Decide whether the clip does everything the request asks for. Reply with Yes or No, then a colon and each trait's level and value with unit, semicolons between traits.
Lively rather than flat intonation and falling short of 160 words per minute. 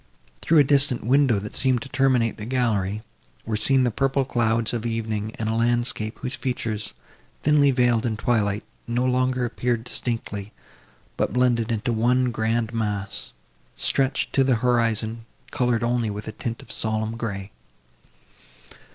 No: narrow, 2.5 semitones; average, 150 wpm